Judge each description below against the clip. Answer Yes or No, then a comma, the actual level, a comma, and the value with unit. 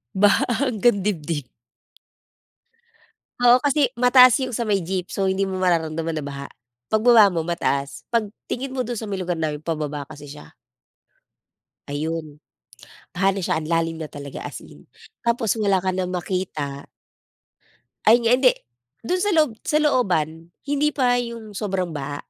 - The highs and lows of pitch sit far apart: Yes, wide, 7.0 semitones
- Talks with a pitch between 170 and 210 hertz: Yes, high, 190 Hz